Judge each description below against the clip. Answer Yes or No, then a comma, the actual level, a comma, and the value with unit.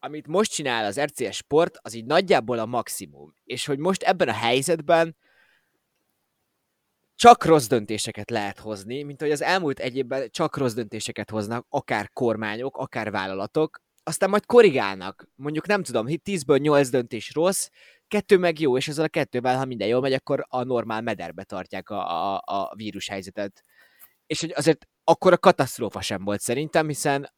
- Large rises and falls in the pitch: Yes, wide, 6.3 semitones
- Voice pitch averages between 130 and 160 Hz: Yes, low, 135 Hz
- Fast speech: Yes, fast, 165 wpm